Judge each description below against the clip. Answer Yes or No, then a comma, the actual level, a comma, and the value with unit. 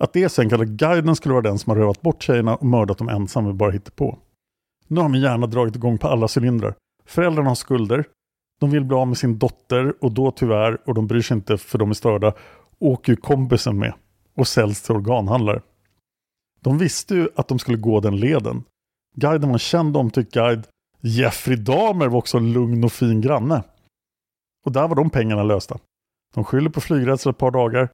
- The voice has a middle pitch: No, low, 125 Hz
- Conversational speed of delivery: No, fast, 210 wpm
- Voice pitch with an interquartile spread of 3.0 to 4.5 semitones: Yes, average, 3.6 semitones